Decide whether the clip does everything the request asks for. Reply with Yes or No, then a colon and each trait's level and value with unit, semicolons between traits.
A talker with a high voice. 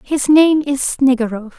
Yes: very high, 270 Hz